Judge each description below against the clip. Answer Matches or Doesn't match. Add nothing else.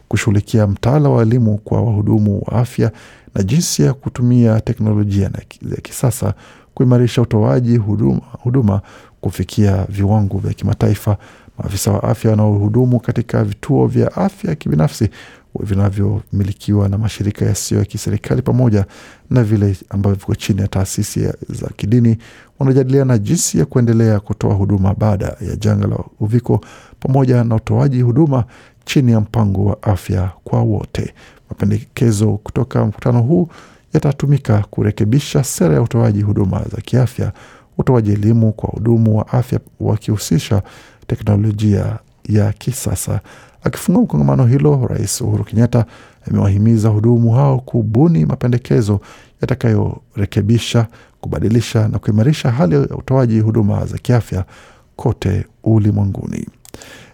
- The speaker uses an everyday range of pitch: Matches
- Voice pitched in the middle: Doesn't match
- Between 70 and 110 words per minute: Doesn't match